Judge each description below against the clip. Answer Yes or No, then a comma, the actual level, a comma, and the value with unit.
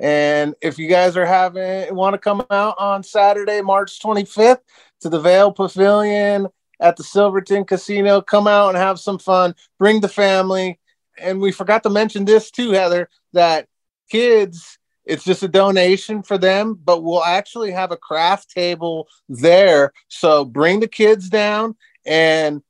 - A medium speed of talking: Yes, average, 160 wpm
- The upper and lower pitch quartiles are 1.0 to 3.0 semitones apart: Yes, average, 2.7 semitones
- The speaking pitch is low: No, high, 195 Hz